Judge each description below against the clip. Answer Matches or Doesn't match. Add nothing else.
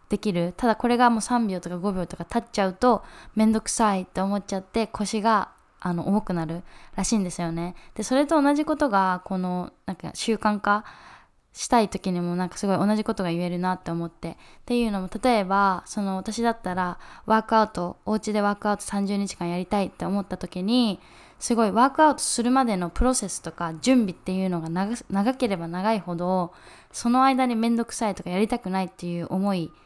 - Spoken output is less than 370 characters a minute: Doesn't match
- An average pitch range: Matches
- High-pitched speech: Matches